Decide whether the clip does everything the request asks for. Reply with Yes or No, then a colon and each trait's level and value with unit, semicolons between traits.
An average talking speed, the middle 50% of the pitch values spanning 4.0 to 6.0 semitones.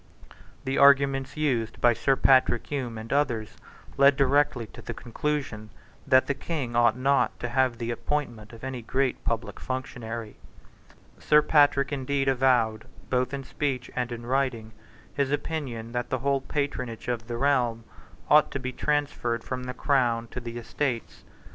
No: average, 160 wpm; average, 2.9 semitones